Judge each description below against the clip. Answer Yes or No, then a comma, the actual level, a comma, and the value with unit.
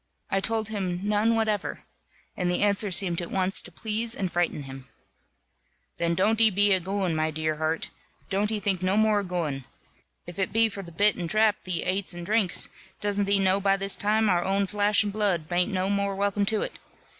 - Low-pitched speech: No, high, 195 Hz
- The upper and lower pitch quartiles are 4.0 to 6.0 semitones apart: No, average, 2.8 semitones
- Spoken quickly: Yes, fast, 215 wpm